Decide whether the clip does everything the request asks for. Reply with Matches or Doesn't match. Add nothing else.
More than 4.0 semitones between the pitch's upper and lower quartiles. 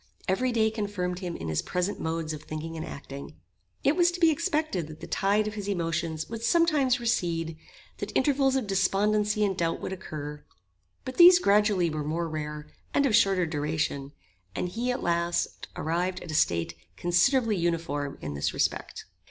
Matches